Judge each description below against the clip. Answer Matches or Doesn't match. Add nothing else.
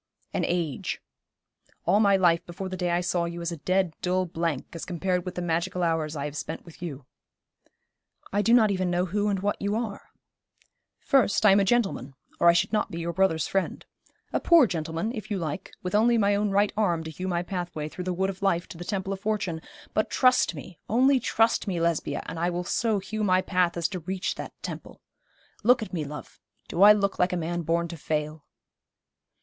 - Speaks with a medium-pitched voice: Matches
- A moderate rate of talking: Doesn't match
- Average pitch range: Matches